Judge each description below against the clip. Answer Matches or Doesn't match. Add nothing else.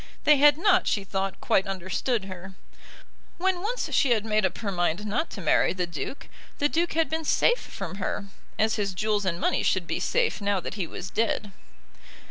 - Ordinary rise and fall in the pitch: Doesn't match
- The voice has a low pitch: Doesn't match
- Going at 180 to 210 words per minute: Matches